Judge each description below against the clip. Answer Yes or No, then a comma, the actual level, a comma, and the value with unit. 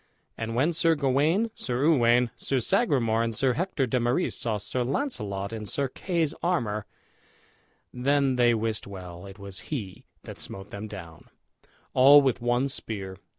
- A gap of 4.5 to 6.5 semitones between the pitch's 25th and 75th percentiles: Yes, average, 4.9 semitones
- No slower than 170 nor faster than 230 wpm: No, average, 155 wpm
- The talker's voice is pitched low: Yes, low, 120 Hz